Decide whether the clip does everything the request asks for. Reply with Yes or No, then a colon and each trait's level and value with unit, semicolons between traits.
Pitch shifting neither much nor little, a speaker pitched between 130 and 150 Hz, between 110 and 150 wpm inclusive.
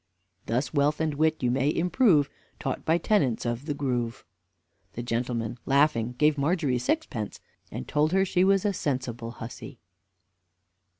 Yes: average, 4.7 semitones; medium, 140 Hz; average, 145 wpm